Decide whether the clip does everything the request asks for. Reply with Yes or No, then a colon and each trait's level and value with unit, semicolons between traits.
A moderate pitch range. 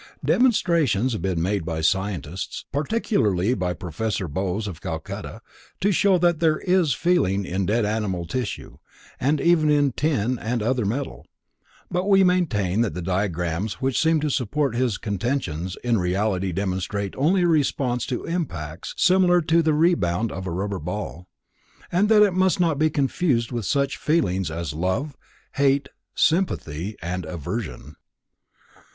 No: wide, 9.0 semitones